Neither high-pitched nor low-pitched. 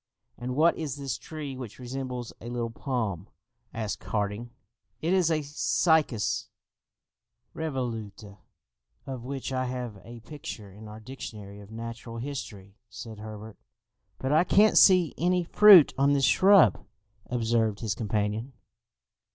No: low, 120 Hz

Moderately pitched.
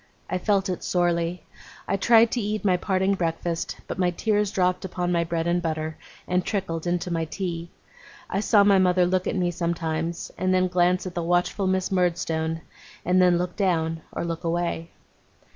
Yes: medium, 180 Hz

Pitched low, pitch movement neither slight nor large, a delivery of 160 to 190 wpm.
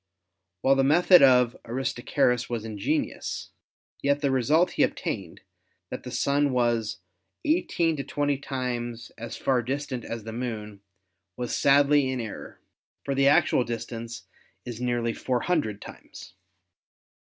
No: low, 125 Hz; average, 3.1 semitones; slow, 135 wpm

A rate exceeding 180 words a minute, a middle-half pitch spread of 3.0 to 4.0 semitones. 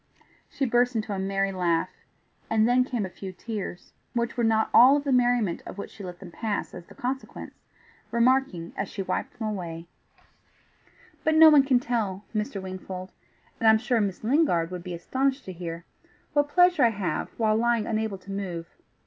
No: average, 190 wpm; average, 4.8 semitones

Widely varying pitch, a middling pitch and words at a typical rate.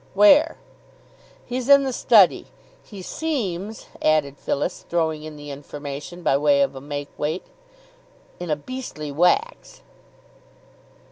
No: wide, 8.6 semitones; medium, 170 Hz; slow, 130 wpm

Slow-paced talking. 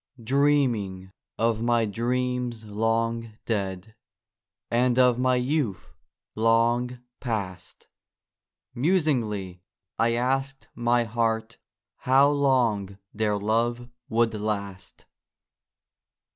Yes: slow, 85 wpm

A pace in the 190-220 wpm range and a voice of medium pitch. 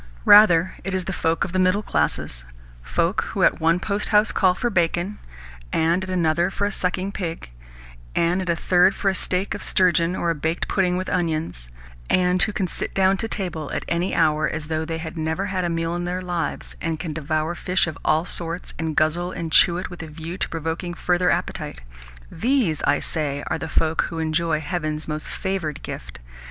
Yes: fast, 205 wpm; medium, 170 Hz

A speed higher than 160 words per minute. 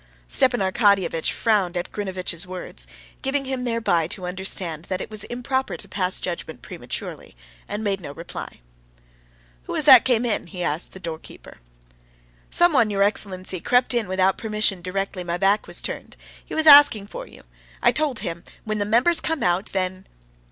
Yes: average, 175 wpm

